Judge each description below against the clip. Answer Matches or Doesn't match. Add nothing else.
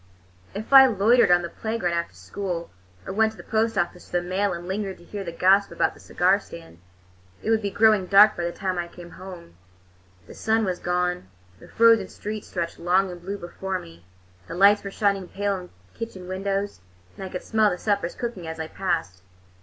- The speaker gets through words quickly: Matches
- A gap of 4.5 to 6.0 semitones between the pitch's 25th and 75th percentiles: Doesn't match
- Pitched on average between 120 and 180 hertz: Doesn't match